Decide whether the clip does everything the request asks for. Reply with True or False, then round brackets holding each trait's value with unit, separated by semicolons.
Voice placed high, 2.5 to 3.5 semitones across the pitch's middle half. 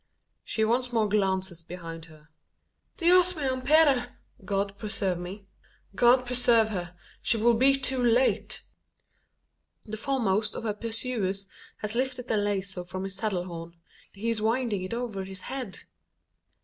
False (215 Hz; 4.5 semitones)